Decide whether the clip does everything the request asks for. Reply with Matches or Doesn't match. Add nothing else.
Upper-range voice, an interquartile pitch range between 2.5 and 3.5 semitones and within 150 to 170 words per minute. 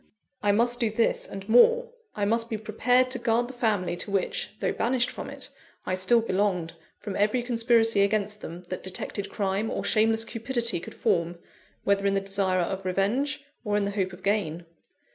Doesn't match